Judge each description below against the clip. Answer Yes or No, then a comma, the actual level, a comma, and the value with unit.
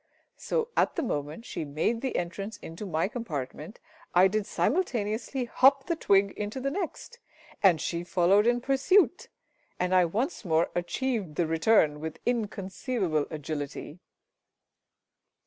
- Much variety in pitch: Yes, wide, 7.2 semitones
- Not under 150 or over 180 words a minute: No, slow, 135 wpm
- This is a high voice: Yes, high, 200 Hz